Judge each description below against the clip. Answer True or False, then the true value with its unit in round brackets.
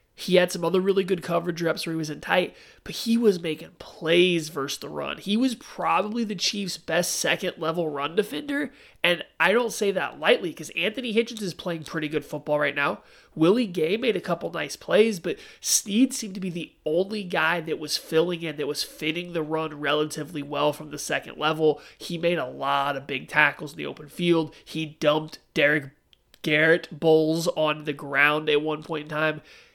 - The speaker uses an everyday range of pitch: True (3.6 semitones)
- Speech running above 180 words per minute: True (200 wpm)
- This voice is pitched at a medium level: True (160 Hz)